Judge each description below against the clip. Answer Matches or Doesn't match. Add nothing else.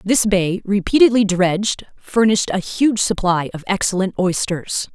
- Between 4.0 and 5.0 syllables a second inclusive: Matches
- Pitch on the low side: Doesn't match